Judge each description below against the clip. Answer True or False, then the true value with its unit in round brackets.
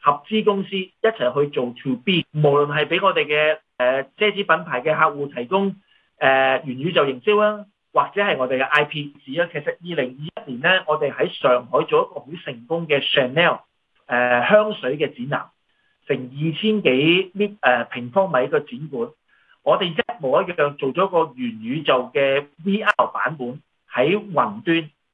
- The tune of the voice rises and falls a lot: True (6.4 semitones)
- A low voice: False (160 Hz)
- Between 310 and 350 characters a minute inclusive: False (265 characters per minute)